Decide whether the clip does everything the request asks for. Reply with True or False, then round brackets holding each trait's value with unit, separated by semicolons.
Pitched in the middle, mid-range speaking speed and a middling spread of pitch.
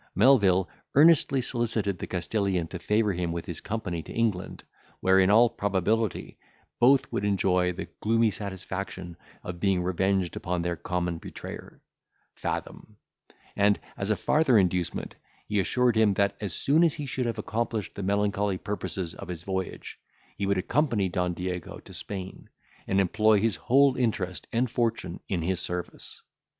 False (100 Hz; 160 wpm; 3.8 semitones)